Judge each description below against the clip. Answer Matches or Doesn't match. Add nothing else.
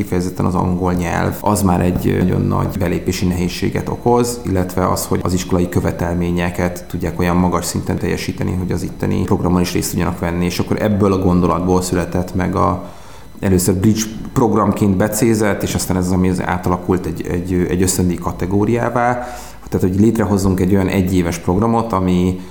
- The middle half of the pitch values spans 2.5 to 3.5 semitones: Doesn't match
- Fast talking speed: Matches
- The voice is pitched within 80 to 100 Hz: Matches